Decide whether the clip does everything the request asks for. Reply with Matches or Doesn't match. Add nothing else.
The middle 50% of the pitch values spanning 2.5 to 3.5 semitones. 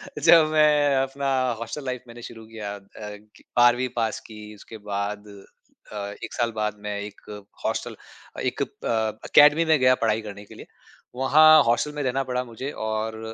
Doesn't match